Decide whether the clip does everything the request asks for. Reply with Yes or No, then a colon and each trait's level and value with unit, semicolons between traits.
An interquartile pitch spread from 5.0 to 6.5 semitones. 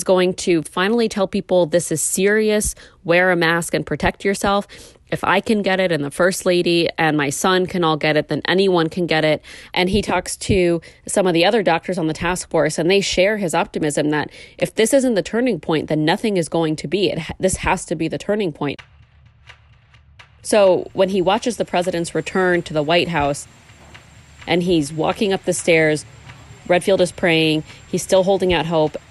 No: average, 3.1 semitones